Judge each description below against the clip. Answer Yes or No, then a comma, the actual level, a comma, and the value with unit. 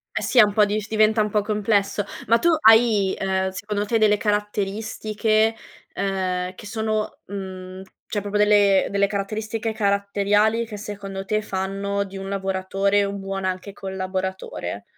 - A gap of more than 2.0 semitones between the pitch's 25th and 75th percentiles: No, narrow, 1.7 semitones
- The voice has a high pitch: Yes, high, 200 Hz